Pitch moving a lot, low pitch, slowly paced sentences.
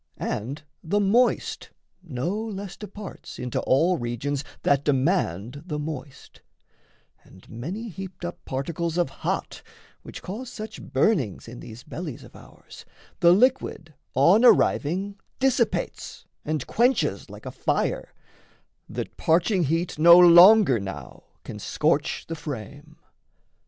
No: wide, 6.5 semitones; medium, 165 Hz; slow, 125 wpm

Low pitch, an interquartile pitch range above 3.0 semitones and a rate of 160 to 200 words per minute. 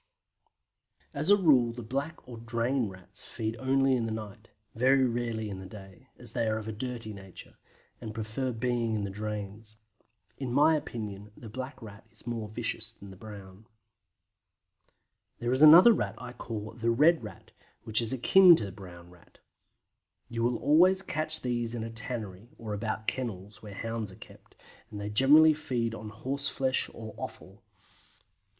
Yes: low, 115 Hz; average, 3.5 semitones; average, 170 wpm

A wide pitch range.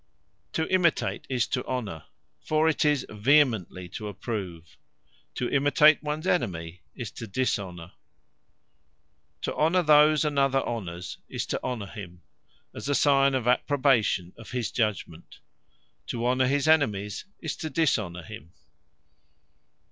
Yes: wide, 7.1 semitones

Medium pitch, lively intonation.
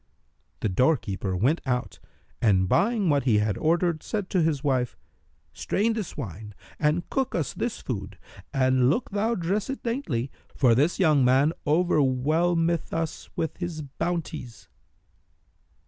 Yes: medium, 150 Hz; wide, 5.9 semitones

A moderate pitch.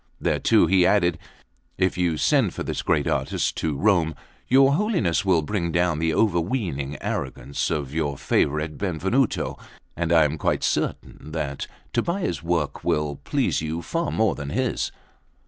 No: very low, 85 Hz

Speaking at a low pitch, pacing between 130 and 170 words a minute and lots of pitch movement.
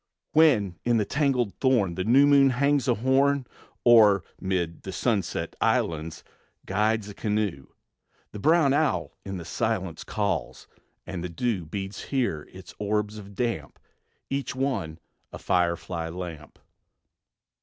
Yes: low, 105 Hz; slow, 135 wpm; wide, 6.0 semitones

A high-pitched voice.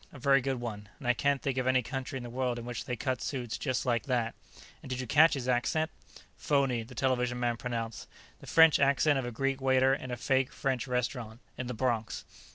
No: low, 130 Hz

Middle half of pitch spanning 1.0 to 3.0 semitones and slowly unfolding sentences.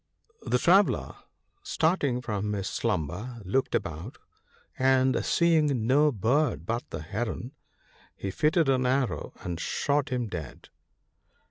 No: wide, 5.6 semitones; slow, 130 wpm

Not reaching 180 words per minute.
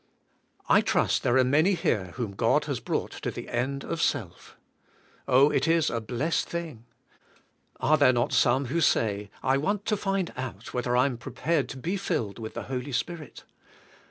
No: average, 185 wpm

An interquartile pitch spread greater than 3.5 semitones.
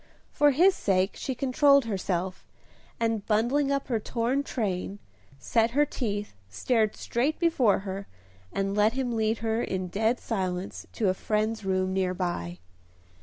Yes: average, 4.7 semitones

